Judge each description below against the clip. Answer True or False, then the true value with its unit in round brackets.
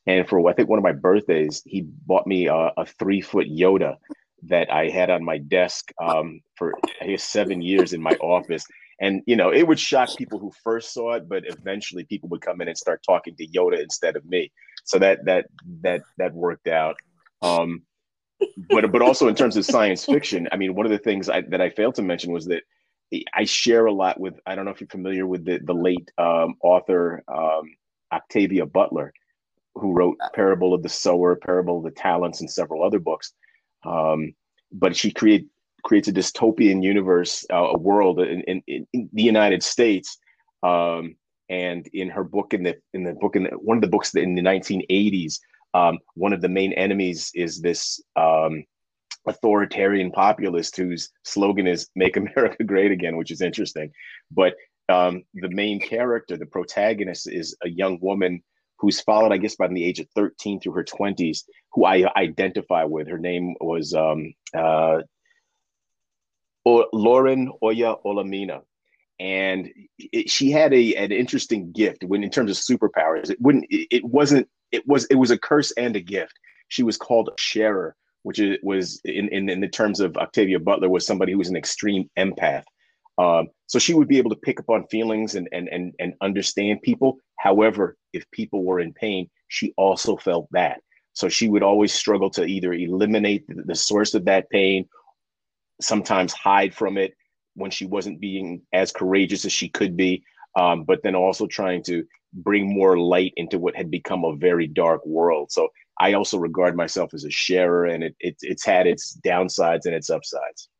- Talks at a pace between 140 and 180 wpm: False (190 wpm)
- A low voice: True (95 Hz)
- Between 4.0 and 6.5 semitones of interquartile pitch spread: False (3.4 semitones)